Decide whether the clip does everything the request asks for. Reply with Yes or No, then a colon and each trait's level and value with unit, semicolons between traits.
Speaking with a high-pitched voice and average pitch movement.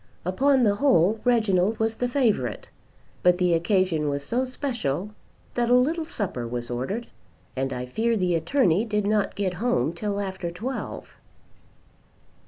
No: high, 200 Hz; wide, 6.0 semitones